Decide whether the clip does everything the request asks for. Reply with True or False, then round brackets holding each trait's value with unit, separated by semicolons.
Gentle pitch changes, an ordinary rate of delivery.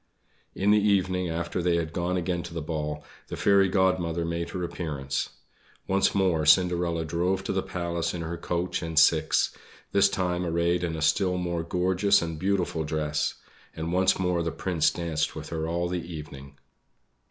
True (2.0 semitones; 175 wpm)